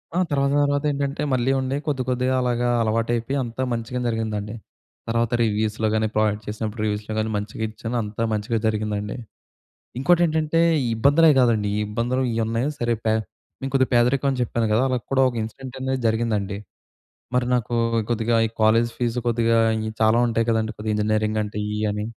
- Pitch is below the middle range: Yes, low, 115 Hz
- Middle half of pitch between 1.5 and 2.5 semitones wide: No, average, 2.9 semitones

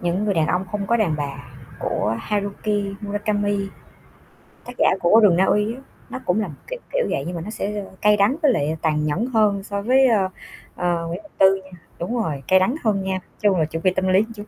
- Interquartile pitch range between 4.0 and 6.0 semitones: No, average, 3.1 semitones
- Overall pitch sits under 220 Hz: Yes, high, 200 Hz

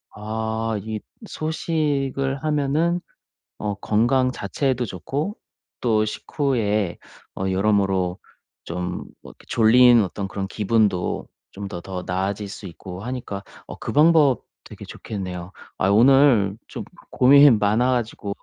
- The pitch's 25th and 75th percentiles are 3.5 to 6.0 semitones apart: Yes, wide, 5.4 semitones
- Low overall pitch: Yes, low, 110 Hz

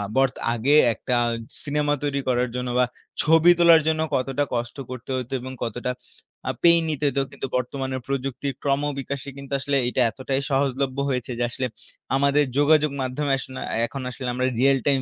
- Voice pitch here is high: No, low, 135 Hz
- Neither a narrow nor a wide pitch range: No, narrow, 2.0 semitones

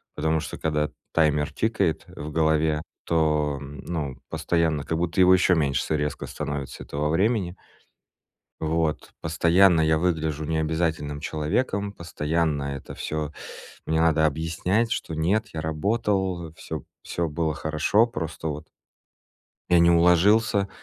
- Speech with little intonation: Yes, narrow, 2.3 semitones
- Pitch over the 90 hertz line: No, very low, 80 Hz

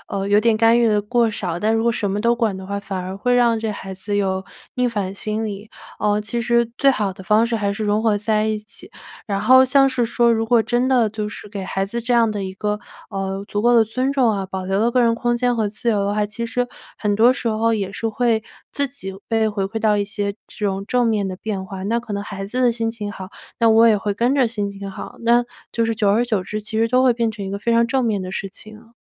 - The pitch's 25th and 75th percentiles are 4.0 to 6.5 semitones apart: No, narrow, 2.6 semitones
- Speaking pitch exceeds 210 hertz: Yes, high, 220 Hz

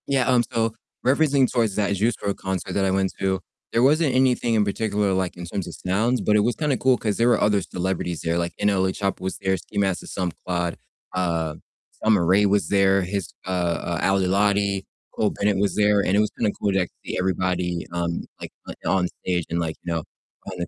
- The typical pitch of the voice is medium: No, very low, 95 Hz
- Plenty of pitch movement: No, average, 2.7 semitones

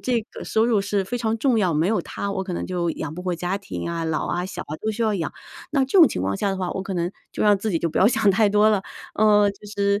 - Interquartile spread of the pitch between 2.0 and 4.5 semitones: Yes, average, 3.4 semitones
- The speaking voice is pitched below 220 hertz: Yes, high, 200 Hz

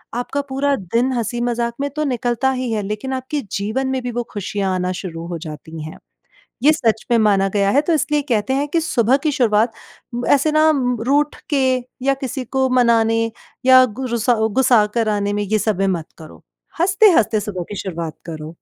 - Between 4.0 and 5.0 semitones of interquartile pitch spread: Yes, average, 4.5 semitones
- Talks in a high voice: Yes, high, 235 Hz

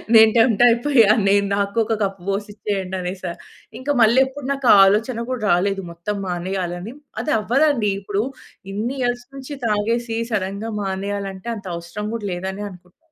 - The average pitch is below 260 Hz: Yes, high, 205 Hz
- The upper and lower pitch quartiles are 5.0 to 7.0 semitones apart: No, average, 3.3 semitones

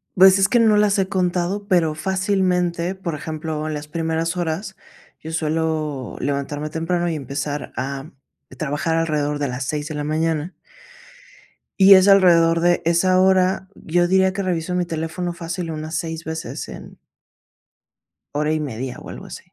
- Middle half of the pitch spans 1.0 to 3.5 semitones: Yes, average, 3.2 semitones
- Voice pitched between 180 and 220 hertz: No, medium, 165 Hz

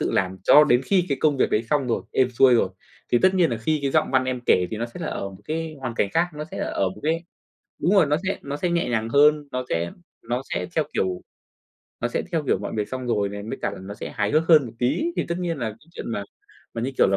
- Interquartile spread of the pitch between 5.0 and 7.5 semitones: Yes, wide, 5.5 semitones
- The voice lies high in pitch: No, low, 130 Hz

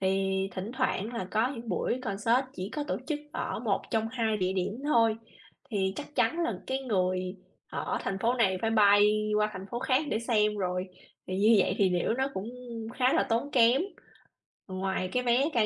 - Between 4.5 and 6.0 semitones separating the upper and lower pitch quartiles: No, average, 3.9 semitones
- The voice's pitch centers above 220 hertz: No, high, 215 Hz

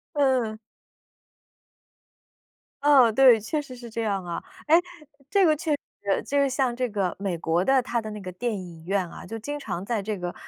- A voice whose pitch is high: Yes, high, 225 Hz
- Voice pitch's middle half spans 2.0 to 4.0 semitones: No, wide, 5.5 semitones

